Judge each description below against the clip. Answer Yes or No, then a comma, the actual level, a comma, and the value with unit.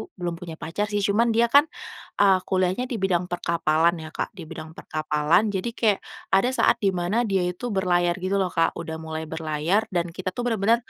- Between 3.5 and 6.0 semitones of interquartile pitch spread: Yes, average, 3.8 semitones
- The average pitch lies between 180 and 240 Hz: Yes, medium, 185 Hz